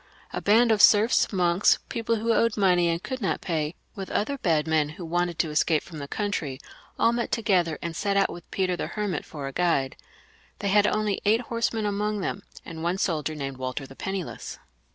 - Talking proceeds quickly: Yes, fast, 215 wpm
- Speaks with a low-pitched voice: No, medium, 185 Hz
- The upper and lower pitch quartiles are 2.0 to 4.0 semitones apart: No, average, 4.7 semitones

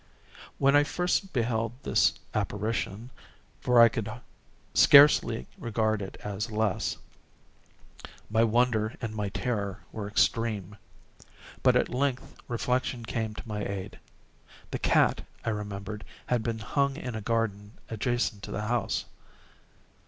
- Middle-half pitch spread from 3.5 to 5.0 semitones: No, average, 2.7 semitones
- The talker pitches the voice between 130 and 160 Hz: No, low, 110 Hz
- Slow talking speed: Yes, slow, 125 wpm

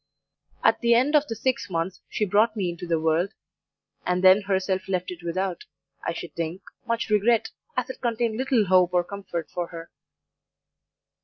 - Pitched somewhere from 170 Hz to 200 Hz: Yes, high, 190 Hz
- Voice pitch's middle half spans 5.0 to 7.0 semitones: No, average, 4.3 semitones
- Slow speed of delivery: No, average, 175 wpm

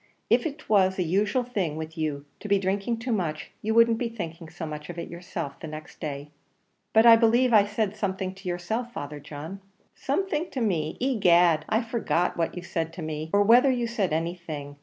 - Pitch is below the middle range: No, medium, 185 Hz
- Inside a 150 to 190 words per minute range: No, fast, 205 wpm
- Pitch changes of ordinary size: No, wide, 6.0 semitones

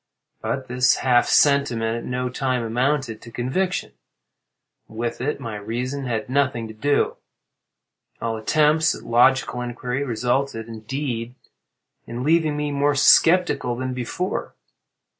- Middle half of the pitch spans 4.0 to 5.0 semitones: No, average, 3.3 semitones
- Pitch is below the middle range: Yes, low, 125 Hz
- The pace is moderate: No, slow, 125 wpm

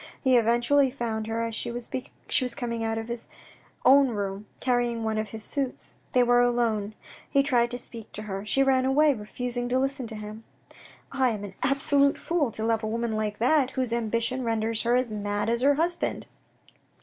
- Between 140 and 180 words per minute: No, average, 195 wpm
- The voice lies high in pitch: Yes, high, 235 Hz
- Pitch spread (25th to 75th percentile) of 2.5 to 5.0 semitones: Yes, average, 2.8 semitones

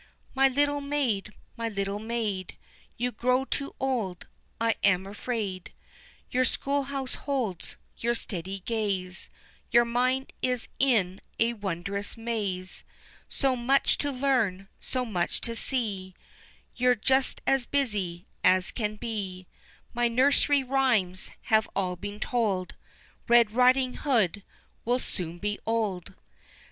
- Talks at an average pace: No, slow, 125 wpm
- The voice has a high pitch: Yes, high, 230 Hz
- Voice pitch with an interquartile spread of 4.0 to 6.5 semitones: Yes, average, 4.7 semitones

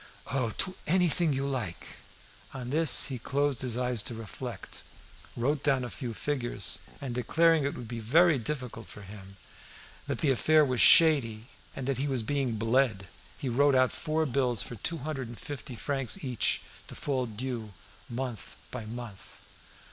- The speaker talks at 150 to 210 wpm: Yes, average, 170 wpm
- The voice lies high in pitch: No, low, 130 Hz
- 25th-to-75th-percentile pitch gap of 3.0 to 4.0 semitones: Yes, average, 3.6 semitones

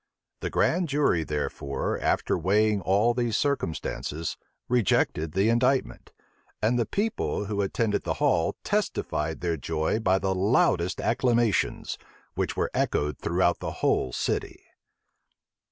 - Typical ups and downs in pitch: No, wide, 6.1 semitones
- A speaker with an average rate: No, slow, 125 wpm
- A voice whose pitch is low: Yes, low, 100 Hz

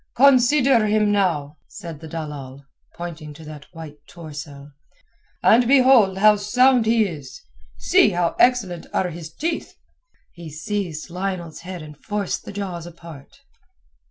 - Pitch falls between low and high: Yes, medium, 175 Hz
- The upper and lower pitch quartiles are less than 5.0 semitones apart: No, wide, 5.5 semitones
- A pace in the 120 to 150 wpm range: Yes, slow, 135 wpm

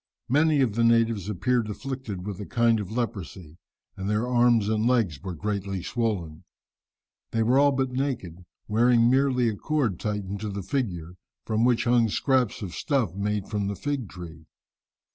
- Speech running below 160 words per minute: No, average, 170 wpm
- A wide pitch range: No, average, 4.1 semitones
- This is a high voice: No, low, 110 Hz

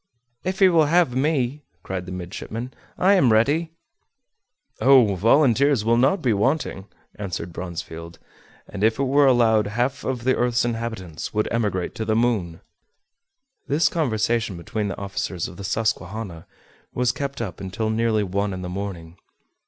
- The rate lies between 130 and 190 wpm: Yes, average, 155 wpm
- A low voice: Yes, low, 115 Hz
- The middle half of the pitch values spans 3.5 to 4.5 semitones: No, average, 5.3 semitones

